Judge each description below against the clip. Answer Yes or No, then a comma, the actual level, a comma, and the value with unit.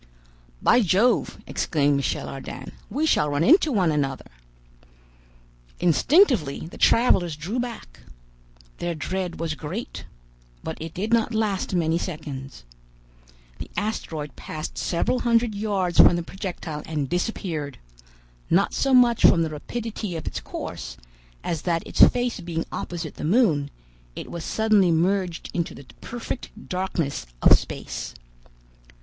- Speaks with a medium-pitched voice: Yes, medium, 175 Hz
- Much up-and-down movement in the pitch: Yes, wide, 5.9 semitones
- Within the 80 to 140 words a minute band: Yes, slow, 135 wpm